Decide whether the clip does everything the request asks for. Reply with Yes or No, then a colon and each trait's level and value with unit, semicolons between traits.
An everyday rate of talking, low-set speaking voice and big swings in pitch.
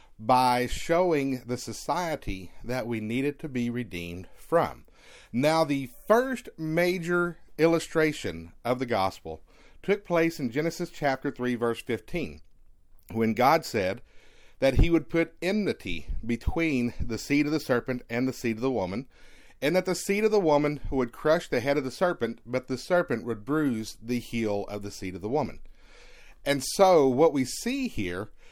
Yes: average, 170 wpm; low, 130 Hz; wide, 6.2 semitones